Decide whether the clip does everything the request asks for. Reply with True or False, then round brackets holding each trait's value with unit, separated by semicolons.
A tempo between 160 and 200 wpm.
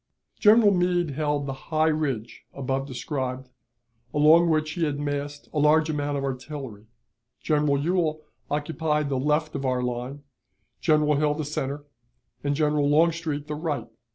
False (150 wpm)